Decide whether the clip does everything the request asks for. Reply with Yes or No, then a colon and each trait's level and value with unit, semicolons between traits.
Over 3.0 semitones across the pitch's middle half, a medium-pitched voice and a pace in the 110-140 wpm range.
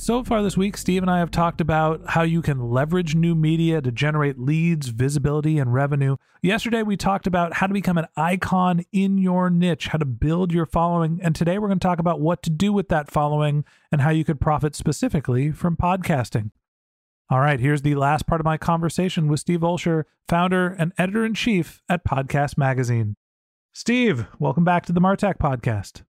No: average, 3.6 semitones; medium, 165 Hz; average, 200 wpm